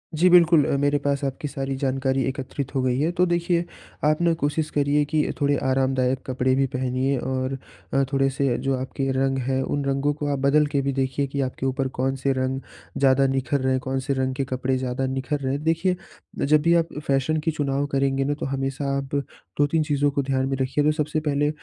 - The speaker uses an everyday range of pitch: No, narrow, 1.7 semitones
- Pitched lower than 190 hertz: Yes, low, 135 Hz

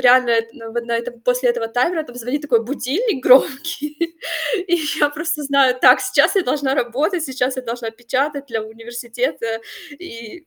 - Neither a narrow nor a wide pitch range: Yes, average, 3.6 semitones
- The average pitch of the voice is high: Yes, very high, 255 Hz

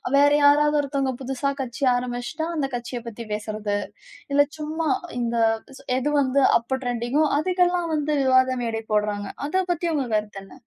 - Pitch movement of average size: Yes, average, 4.0 semitones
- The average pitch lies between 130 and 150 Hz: No, very high, 265 Hz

